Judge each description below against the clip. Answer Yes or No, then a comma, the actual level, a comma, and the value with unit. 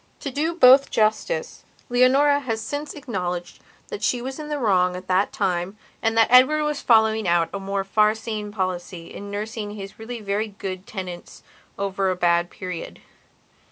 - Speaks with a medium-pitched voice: No, high, 215 Hz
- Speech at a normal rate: Yes, average, 170 wpm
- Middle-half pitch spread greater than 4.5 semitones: Yes, average, 5.2 semitones